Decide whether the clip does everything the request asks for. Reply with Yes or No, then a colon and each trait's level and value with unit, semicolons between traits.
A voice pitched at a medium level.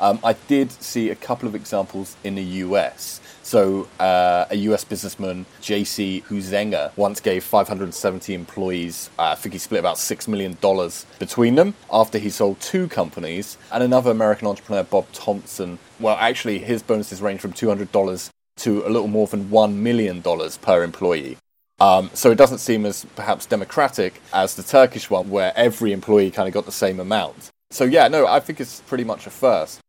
No: low, 105 Hz